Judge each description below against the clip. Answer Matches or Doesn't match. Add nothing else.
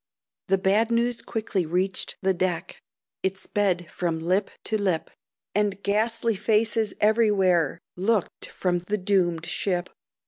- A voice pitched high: Matches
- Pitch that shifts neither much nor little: Matches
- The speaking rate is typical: Doesn't match